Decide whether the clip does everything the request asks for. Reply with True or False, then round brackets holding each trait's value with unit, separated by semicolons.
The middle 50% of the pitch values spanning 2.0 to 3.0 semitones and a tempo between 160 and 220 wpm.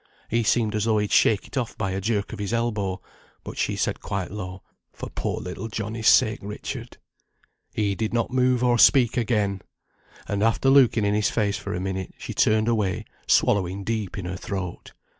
True (2.7 semitones; 195 wpm)